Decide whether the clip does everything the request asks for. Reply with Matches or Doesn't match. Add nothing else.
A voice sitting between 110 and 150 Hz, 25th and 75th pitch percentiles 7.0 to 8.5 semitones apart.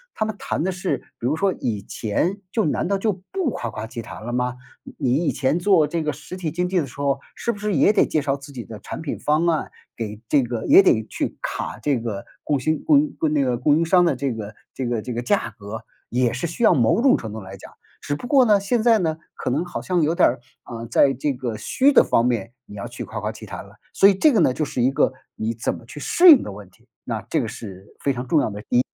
Matches